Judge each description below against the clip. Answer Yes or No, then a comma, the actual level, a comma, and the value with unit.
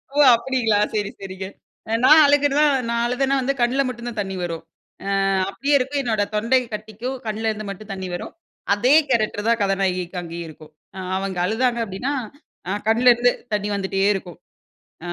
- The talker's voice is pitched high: Yes, high, 220 Hz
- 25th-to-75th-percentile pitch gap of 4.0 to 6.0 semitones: Yes, average, 4.3 semitones